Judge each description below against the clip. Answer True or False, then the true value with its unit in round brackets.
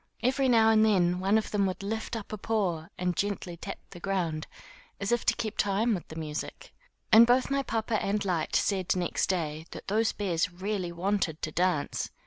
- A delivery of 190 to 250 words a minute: True (200 wpm)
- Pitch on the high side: True (195 Hz)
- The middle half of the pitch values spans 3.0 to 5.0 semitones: True (3.9 semitones)